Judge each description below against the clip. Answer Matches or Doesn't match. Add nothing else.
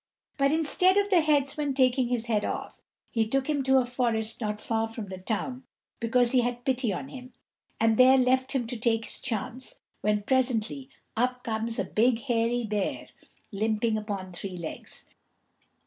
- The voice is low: Doesn't match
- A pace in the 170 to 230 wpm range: Matches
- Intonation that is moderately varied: Matches